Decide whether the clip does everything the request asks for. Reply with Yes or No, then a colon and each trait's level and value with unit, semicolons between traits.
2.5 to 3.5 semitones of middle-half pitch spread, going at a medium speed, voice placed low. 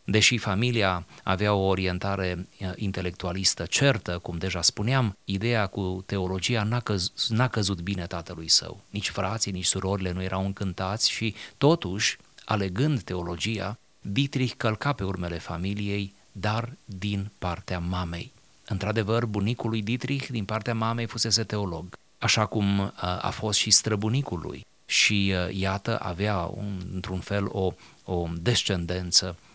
Yes: average, 3.2 semitones; average, 130 wpm; low, 100 Hz